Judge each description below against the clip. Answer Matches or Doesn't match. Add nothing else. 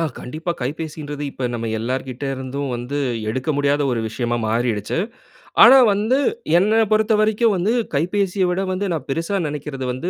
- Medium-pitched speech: Matches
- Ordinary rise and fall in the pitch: Doesn't match